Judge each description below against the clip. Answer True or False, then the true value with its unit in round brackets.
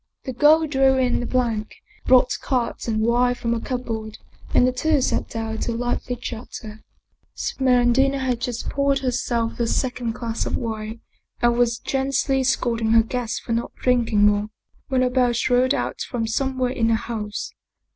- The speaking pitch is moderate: False (245 Hz)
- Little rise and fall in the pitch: True (2.2 semitones)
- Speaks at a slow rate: False (170 wpm)